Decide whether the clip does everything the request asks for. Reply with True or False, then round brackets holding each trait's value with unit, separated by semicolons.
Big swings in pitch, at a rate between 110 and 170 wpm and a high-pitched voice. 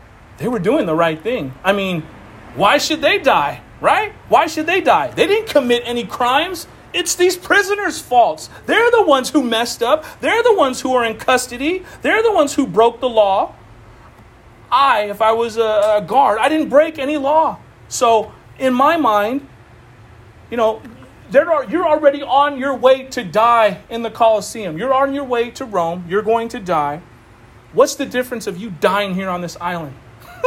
False (7.5 semitones; 185 wpm; 235 Hz)